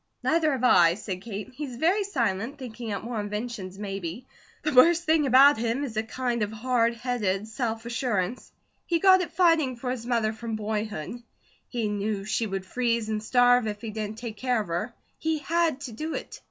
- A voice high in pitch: Yes, high, 235 Hz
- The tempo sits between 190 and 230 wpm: Yes, average, 195 wpm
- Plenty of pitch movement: No, average, 3.5 semitones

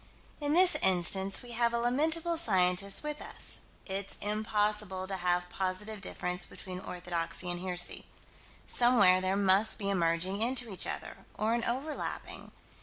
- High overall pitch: Yes, high, 200 Hz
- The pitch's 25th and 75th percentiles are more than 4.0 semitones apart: Yes, average, 4.4 semitones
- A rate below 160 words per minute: Yes, average, 150 wpm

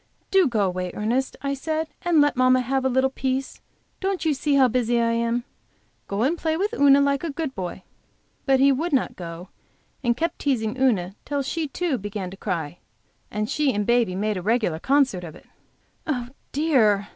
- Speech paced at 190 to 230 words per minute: Yes, average, 195 wpm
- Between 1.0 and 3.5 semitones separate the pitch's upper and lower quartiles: No, average, 5.2 semitones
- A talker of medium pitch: No, very high, 255 Hz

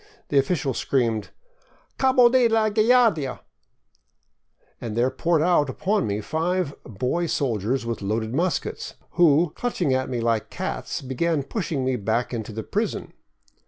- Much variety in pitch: Yes, wide, 7.3 semitones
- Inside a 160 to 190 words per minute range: No, average, 150 wpm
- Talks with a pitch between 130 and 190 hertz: Yes, medium, 140 Hz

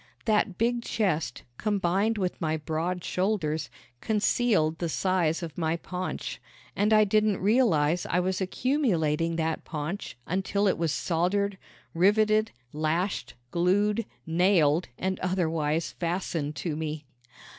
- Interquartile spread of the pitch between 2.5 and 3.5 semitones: No, average, 4.1 semitones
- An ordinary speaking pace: No, slow, 125 wpm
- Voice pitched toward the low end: No, medium, 180 Hz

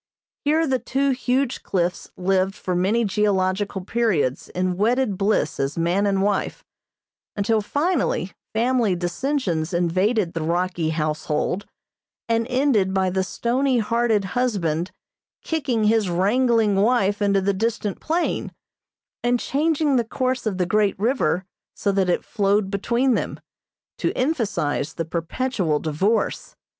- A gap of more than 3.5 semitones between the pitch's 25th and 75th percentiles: Yes, average, 4.8 semitones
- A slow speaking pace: Yes, slow, 130 wpm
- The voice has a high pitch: Yes, high, 205 Hz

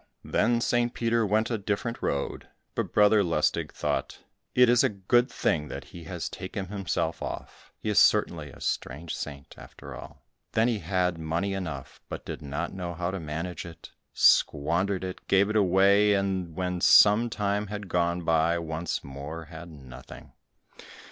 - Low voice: Yes, very low, 90 Hz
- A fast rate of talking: No, average, 170 wpm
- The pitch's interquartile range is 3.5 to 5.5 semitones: Yes, average, 4.0 semitones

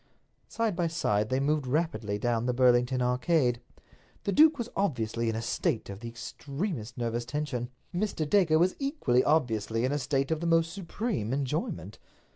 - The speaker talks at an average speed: Yes, average, 170 wpm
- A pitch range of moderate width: No, wide, 6.0 semitones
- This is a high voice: No, low, 135 Hz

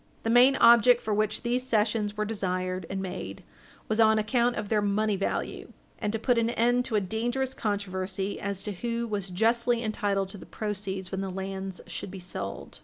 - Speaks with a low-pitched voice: No, high, 210 Hz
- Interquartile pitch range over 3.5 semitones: No, average, 3.2 semitones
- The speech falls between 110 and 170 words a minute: No, average, 195 wpm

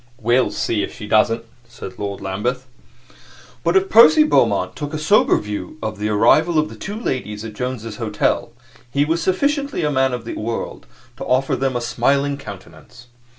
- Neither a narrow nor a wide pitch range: No, wide, 5.9 semitones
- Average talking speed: Yes, average, 180 wpm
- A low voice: Yes, low, 125 Hz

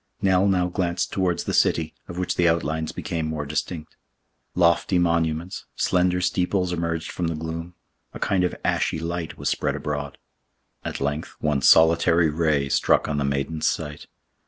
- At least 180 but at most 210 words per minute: No, average, 160 wpm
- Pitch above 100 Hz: No, very low, 85 Hz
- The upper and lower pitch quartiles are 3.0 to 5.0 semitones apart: No, narrow, 2.4 semitones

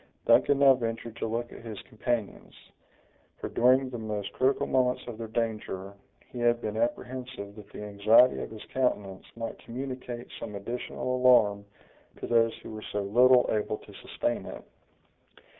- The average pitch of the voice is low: Yes, low, 115 Hz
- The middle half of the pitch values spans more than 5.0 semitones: No, average, 2.9 semitones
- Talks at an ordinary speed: Yes, average, 160 wpm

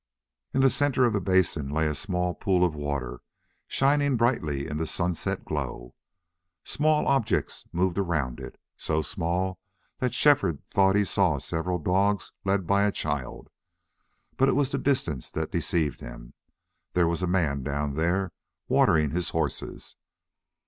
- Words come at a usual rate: Yes, average, 155 wpm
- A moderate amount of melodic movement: Yes, average, 5.0 semitones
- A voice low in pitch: Yes, very low, 90 Hz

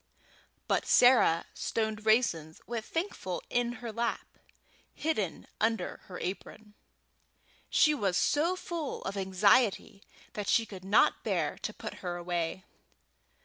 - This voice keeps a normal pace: No, slow, 125 wpm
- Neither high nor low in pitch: No, high, 215 Hz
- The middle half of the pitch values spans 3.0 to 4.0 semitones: No, average, 4.5 semitones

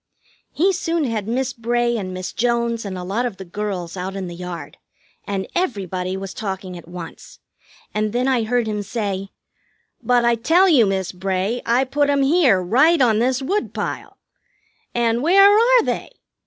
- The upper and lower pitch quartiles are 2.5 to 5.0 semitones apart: No, wide, 5.4 semitones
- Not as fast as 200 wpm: Yes, average, 175 wpm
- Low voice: No, high, 230 Hz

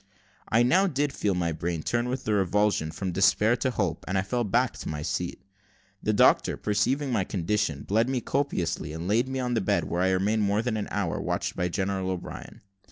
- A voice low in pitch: Yes, low, 105 Hz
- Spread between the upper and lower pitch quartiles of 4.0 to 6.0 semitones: Yes, average, 4.9 semitones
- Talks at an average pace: No, fast, 215 wpm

